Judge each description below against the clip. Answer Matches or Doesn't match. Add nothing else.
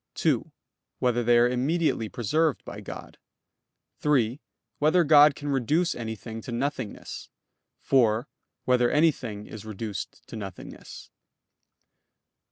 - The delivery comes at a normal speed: Doesn't match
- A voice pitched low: Matches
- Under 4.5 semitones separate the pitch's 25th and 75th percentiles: Doesn't match